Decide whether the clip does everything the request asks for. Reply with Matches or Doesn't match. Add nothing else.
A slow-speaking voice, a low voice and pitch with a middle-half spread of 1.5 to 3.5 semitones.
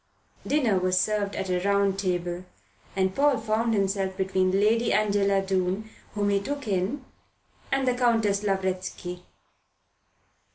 Doesn't match